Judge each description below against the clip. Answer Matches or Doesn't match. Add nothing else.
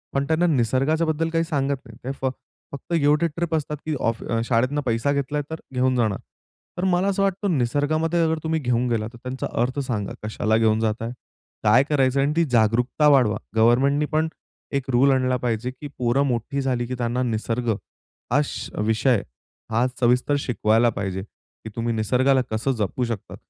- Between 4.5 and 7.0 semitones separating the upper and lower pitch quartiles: Doesn't match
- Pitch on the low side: Matches